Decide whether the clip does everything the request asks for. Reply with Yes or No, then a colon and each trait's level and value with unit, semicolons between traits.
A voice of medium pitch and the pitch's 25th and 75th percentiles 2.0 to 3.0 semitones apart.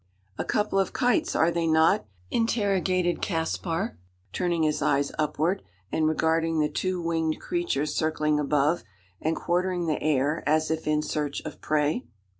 Yes: medium, 160 Hz; narrow, 2.6 semitones